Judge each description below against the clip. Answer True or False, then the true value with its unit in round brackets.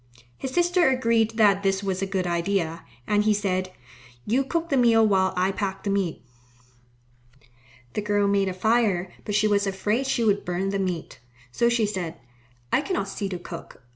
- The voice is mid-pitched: False (200 Hz)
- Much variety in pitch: False (3.1 semitones)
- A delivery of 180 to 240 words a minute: True (185 wpm)